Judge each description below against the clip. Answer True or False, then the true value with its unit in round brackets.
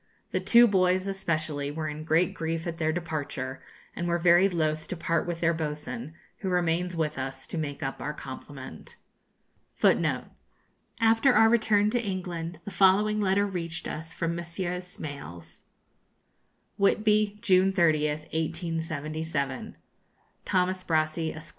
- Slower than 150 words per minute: True (140 wpm)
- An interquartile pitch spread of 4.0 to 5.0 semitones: False (3.3 semitones)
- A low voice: False (165 Hz)